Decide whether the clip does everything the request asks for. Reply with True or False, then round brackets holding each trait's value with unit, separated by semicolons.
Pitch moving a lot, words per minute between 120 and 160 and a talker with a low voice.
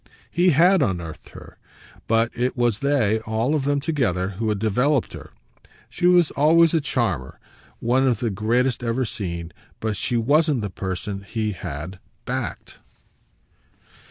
True (5.9 semitones; 150 wpm; 115 Hz)